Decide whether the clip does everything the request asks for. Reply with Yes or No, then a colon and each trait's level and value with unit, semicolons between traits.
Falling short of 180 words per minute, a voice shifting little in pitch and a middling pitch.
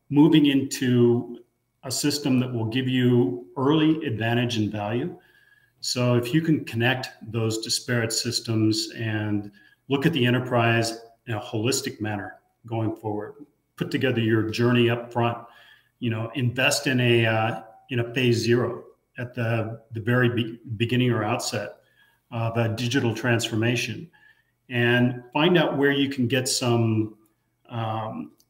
No: average, 145 wpm; narrow, 2.1 semitones; low, 120 Hz